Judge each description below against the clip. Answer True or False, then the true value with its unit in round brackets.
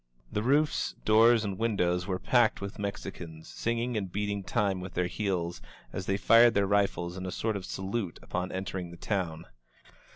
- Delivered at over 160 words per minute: True (175 wpm)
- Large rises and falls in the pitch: False (3.1 semitones)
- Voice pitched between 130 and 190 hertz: False (100 Hz)